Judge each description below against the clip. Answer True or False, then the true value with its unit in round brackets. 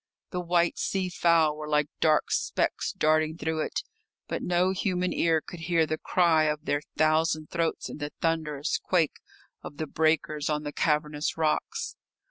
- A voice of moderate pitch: True (160 Hz)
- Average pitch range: False (2.0 semitones)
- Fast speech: False (165 wpm)